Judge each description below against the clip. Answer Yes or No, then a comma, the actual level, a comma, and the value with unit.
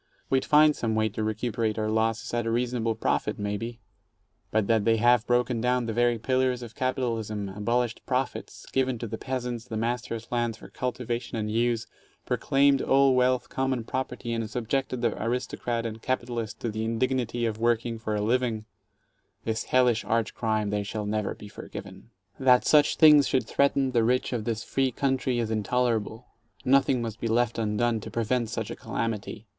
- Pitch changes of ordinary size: No, narrow, 2.2 semitones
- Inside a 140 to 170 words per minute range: No, average, 185 wpm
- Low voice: Yes, low, 115 Hz